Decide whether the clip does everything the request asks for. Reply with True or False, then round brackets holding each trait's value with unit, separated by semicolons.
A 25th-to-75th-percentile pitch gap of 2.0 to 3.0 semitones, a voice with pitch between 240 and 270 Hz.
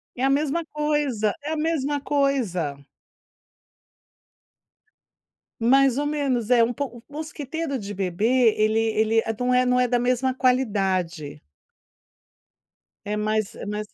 False (4.7 semitones; 250 Hz)